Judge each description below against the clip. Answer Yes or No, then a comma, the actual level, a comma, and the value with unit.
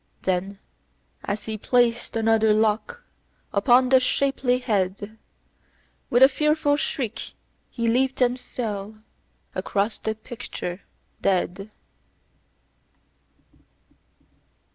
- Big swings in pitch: No, average, 3.6 semitones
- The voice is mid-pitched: No, high, 225 Hz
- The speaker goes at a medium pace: No, slow, 90 wpm